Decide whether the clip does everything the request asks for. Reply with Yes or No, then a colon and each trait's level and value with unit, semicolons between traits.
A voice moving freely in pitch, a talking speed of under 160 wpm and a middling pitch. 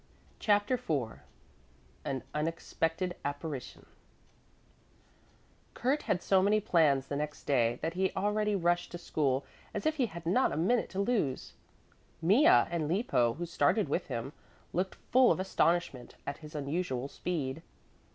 Yes: wide, 5.8 semitones; average, 140 wpm; medium, 170 Hz